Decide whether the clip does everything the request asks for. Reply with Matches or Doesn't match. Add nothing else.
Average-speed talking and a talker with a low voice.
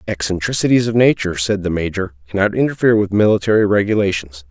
Matches